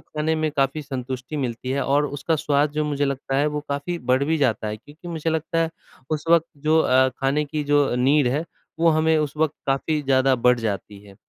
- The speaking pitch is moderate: Yes, medium, 145 Hz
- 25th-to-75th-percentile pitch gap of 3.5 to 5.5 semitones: No, average, 2.8 semitones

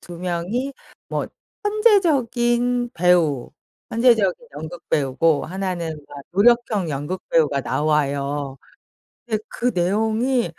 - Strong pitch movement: Yes, wide, 7.8 semitones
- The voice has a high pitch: No, medium, 180 Hz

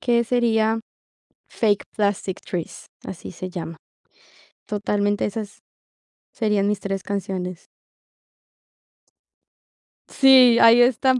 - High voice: Yes, high, 210 Hz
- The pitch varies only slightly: No, average, 3.3 semitones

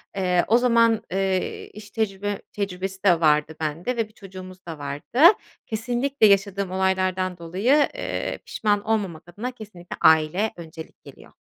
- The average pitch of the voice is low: No, high, 190 Hz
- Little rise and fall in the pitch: No, average, 3.6 semitones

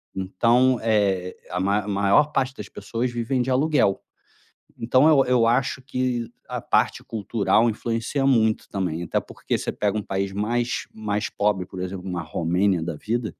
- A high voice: No, low, 110 Hz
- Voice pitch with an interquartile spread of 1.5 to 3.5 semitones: No, average, 4.1 semitones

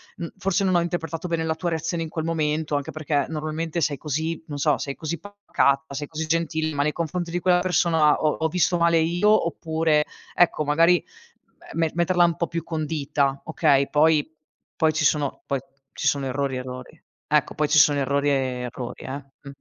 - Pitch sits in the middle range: Yes, medium, 160 Hz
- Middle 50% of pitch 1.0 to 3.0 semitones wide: Yes, narrow, 2.4 semitones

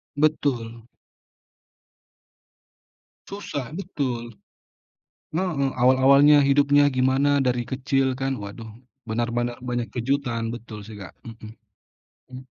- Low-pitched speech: Yes, low, 130 Hz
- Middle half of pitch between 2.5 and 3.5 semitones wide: Yes, average, 3.2 semitones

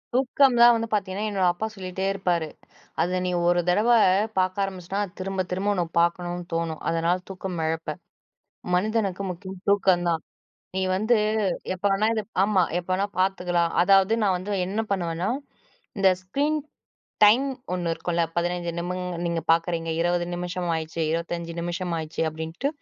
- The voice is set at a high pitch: No, medium, 180 Hz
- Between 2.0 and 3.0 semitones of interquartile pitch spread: Yes, narrow, 2.4 semitones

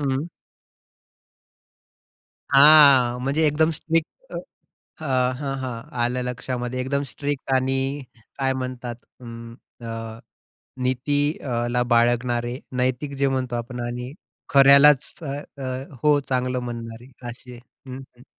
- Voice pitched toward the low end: Yes, low, 125 Hz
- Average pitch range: No, narrow, 2.3 semitones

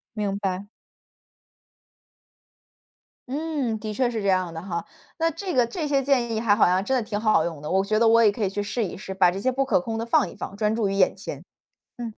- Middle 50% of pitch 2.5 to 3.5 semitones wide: No, average, 4.2 semitones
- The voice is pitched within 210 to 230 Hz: Yes, high, 215 Hz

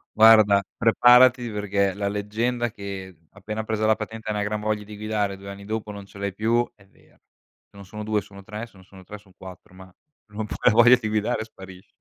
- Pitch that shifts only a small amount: Yes, narrow, 1.8 semitones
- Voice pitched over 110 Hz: No, low, 105 Hz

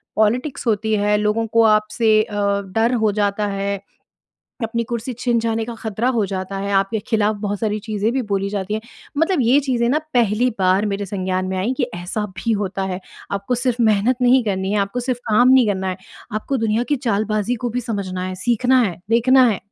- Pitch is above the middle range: Yes, high, 215 Hz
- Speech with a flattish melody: No, average, 3.3 semitones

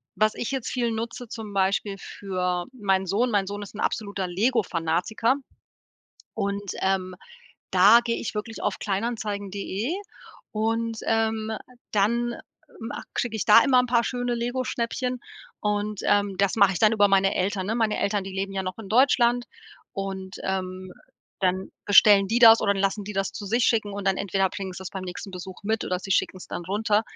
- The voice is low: No, high, 205 Hz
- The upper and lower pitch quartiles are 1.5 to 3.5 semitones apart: Yes, average, 2.8 semitones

